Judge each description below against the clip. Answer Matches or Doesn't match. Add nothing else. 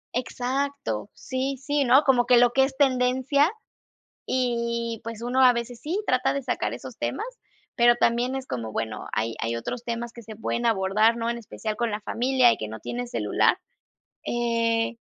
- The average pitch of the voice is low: Doesn't match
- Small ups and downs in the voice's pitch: Matches